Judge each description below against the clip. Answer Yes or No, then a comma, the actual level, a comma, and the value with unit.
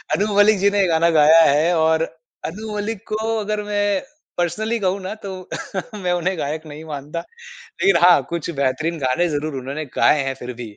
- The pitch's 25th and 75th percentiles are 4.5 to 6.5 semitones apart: Yes, average, 4.8 semitones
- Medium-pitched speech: Yes, medium, 170 Hz